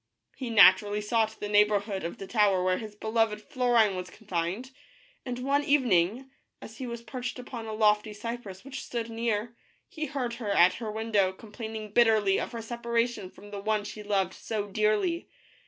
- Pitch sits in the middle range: No, high, 220 Hz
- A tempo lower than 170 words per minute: No, average, 175 wpm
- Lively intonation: No, narrow, 2.4 semitones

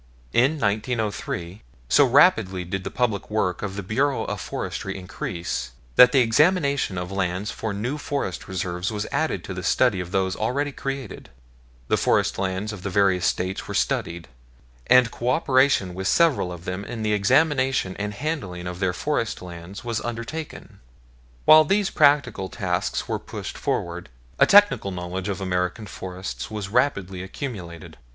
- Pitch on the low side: Yes, low, 100 Hz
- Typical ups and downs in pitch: No, wide, 5.9 semitones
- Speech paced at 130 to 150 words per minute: No, average, 160 wpm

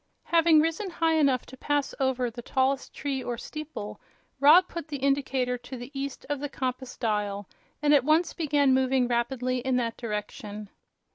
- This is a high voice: Yes, very high, 265 Hz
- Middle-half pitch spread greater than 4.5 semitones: No, average, 3.0 semitones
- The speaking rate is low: No, average, 170 wpm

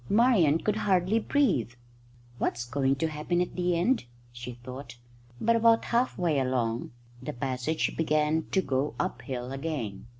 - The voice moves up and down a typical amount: No, wide, 6.4 semitones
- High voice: No, medium, 155 Hz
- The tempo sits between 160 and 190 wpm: No, average, 145 wpm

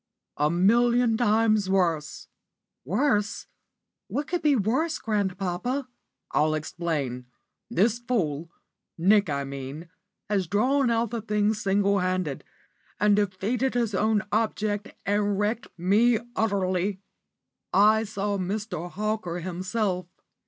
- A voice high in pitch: Yes, high, 205 Hz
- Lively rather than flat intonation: No, average, 3.6 semitones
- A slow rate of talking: Yes, slow, 110 wpm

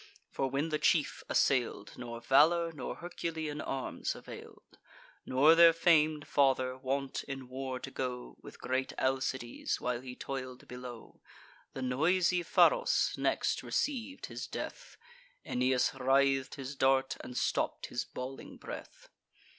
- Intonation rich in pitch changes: No, average, 3.3 semitones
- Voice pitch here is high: No, low, 135 Hz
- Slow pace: Yes, slow, 130 wpm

